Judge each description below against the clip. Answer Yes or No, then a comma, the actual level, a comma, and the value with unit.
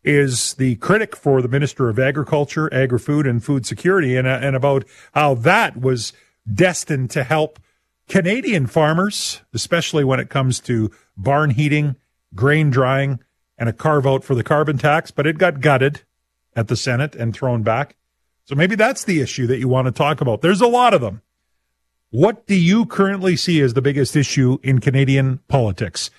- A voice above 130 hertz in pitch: Yes, medium, 140 Hz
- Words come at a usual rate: Yes, average, 180 wpm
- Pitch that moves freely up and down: No, average, 3.4 semitones